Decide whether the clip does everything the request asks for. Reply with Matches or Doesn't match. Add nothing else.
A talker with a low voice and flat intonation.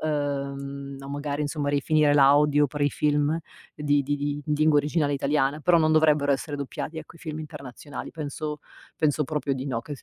Doesn't match